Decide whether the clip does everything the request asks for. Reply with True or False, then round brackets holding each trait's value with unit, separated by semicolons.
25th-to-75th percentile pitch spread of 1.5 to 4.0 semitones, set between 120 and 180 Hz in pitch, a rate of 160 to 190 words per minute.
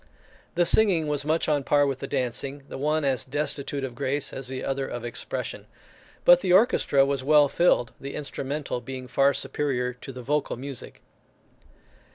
True (2.4 semitones; 140 Hz; 180 wpm)